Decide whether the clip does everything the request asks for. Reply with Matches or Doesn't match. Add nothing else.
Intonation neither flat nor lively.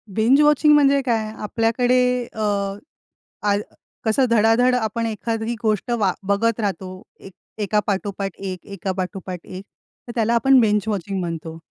Matches